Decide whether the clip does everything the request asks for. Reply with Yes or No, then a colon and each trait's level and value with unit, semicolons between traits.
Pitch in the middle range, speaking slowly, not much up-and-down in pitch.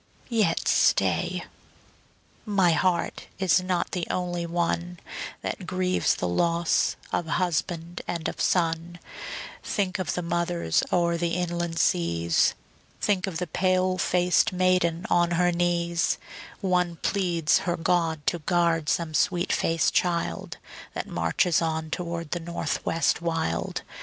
Yes: medium, 175 Hz; slow, 130 wpm; narrow, 1.4 semitones